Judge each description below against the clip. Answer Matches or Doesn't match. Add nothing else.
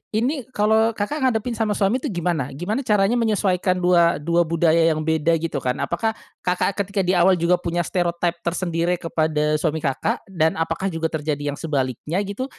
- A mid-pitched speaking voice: Matches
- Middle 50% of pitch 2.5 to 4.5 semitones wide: Matches